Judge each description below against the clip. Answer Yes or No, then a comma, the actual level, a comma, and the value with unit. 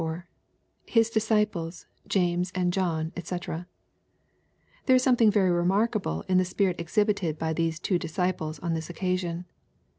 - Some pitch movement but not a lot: Yes, average, 3.4 semitones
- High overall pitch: No, medium, 180 Hz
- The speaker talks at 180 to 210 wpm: No, average, 140 wpm